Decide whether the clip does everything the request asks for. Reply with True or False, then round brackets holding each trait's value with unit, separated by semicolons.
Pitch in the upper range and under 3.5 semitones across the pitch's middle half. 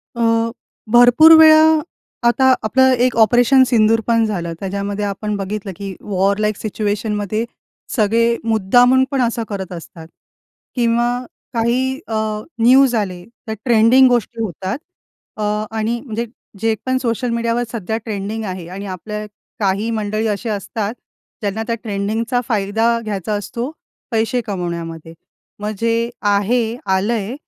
True (220 Hz; 2.8 semitones)